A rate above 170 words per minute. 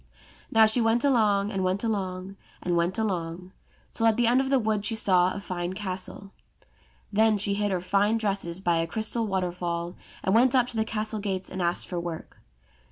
Yes: average, 200 wpm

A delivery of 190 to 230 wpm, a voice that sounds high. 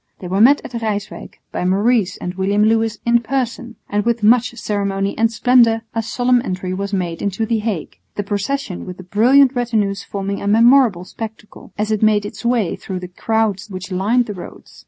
Yes: average, 195 wpm; high, 215 Hz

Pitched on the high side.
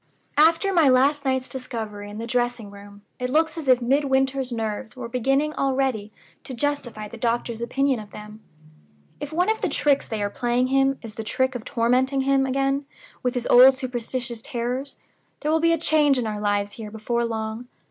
Yes: very high, 255 Hz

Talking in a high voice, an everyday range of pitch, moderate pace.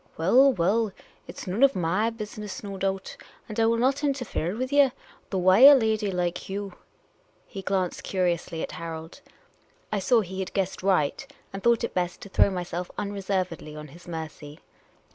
Yes: high, 195 Hz; average, 4.1 semitones; average, 185 wpm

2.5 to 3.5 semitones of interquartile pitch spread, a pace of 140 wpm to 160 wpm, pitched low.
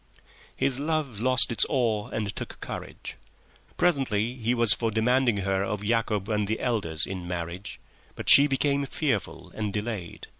No: average, 4.0 semitones; average, 155 wpm; low, 110 Hz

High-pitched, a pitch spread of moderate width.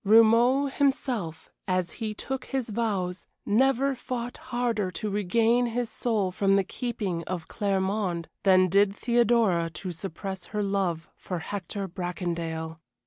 Yes: high, 200 Hz; average, 4.5 semitones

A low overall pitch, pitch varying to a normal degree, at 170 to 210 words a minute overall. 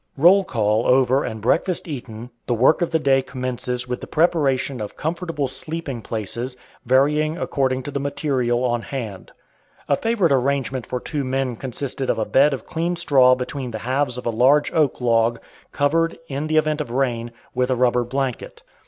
Yes: low, 130 Hz; average, 3.3 semitones; average, 180 wpm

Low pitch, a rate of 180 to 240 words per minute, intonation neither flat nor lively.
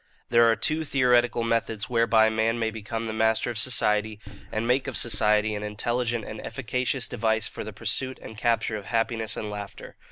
No: low, 115 Hz; average, 185 wpm; narrow, 1.7 semitones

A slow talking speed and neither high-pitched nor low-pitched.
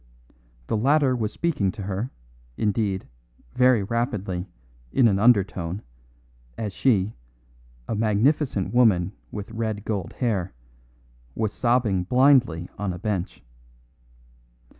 No: slow, 110 wpm; low, 105 Hz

